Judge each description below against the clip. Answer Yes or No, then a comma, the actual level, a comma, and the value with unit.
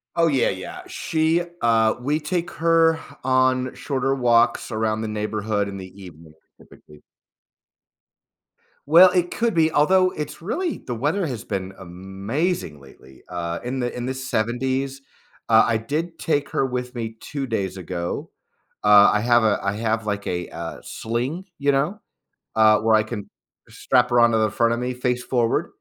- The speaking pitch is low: Yes, low, 120 Hz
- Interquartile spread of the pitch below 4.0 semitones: No, average, 5.0 semitones